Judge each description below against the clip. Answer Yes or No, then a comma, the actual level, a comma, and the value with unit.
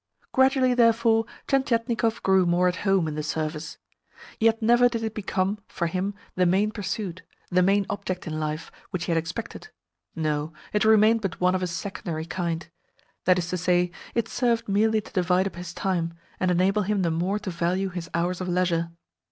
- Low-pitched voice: No, medium, 185 Hz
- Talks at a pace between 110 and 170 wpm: No, average, 190 wpm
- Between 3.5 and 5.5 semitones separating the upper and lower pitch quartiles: Yes, average, 3.8 semitones